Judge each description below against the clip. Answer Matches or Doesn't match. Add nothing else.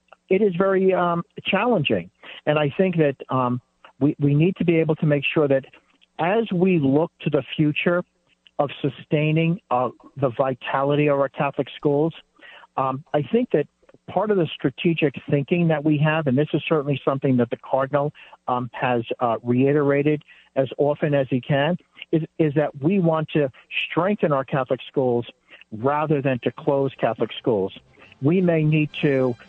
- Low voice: Doesn't match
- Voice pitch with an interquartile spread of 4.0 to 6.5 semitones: Doesn't match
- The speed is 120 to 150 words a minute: Doesn't match